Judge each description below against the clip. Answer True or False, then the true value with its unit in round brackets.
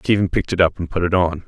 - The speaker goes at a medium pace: False (325 wpm)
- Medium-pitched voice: False (90 Hz)